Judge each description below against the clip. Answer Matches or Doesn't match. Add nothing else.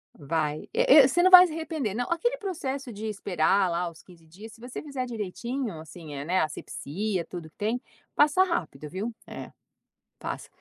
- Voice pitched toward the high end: Matches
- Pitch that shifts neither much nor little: Doesn't match